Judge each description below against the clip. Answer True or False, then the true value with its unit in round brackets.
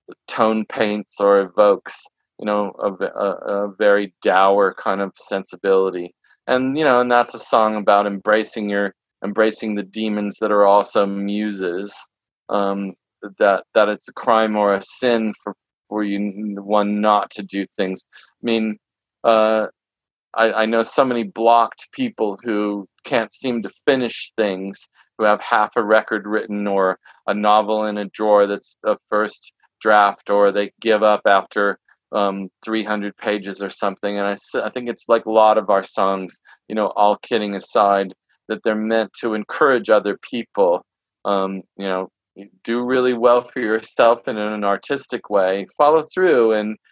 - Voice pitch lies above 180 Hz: False (105 Hz)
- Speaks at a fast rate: False (165 wpm)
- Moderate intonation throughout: False (1.8 semitones)